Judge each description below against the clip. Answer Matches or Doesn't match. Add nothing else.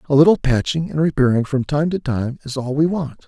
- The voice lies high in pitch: Doesn't match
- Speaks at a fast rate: Matches